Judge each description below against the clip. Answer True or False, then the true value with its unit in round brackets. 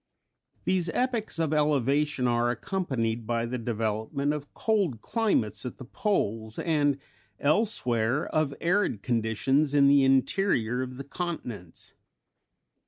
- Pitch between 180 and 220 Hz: False (140 Hz)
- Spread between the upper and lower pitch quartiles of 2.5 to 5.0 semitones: False (5.5 semitones)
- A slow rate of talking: True (120 wpm)